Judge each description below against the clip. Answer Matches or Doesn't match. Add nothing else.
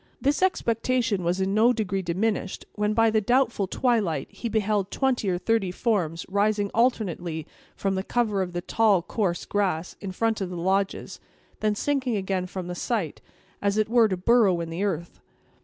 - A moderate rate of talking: Matches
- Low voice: Doesn't match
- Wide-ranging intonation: Doesn't match